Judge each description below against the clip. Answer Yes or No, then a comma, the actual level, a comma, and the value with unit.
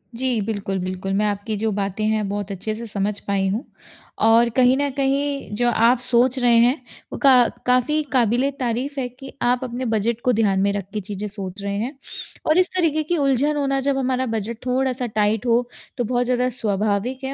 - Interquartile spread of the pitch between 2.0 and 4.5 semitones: Yes, average, 3.9 semitones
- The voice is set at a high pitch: Yes, high, 235 Hz